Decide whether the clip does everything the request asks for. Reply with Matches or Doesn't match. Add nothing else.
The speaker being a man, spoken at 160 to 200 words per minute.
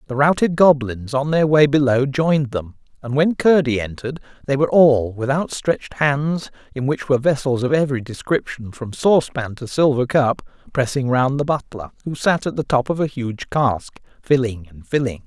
Matches